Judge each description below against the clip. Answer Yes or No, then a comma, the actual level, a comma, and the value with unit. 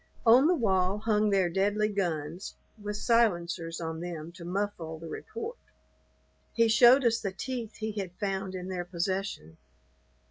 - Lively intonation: No, average, 4.1 semitones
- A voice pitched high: Yes, high, 195 Hz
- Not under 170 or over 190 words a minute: No, average, 150 wpm